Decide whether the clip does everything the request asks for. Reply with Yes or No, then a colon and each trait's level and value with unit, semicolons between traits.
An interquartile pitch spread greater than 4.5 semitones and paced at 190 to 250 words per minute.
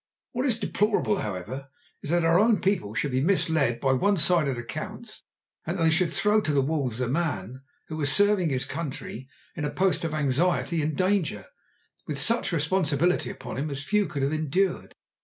Yes: average, 5.1 semitones; average, 195 wpm